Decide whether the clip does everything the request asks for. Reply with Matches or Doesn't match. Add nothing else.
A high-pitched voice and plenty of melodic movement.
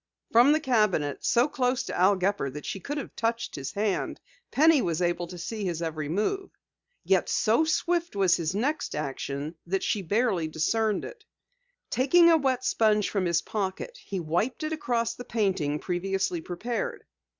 Matches